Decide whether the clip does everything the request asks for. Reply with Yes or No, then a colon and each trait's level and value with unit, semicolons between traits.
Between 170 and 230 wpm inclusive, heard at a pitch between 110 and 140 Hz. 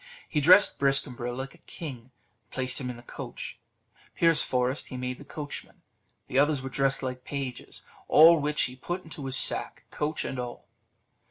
Yes: average, 175 wpm; low, 135 Hz